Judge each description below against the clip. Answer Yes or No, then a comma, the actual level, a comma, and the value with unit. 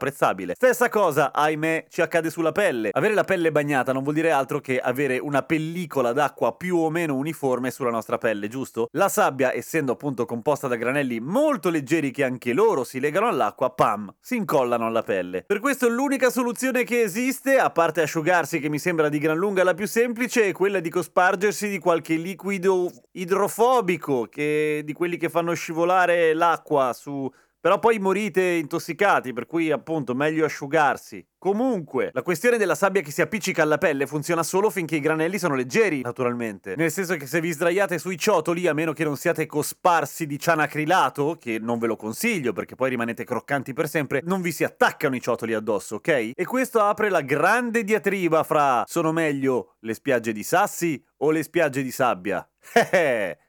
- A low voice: No, medium, 165 Hz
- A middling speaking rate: No, fast, 185 wpm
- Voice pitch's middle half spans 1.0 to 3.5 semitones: No, average, 5.1 semitones